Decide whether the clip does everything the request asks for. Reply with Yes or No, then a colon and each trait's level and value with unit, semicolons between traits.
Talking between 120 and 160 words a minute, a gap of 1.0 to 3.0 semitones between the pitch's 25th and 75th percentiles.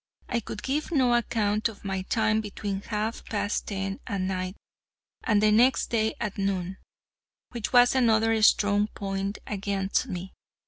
Yes: average, 150 wpm; narrow, 2.5 semitones